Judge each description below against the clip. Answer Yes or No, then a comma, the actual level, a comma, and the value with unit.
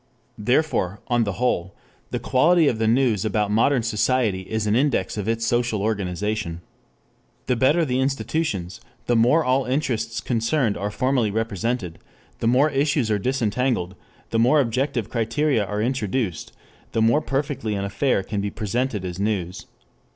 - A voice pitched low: Yes, low, 115 Hz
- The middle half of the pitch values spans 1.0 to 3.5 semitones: No, average, 4.0 semitones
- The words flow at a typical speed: Yes, average, 155 wpm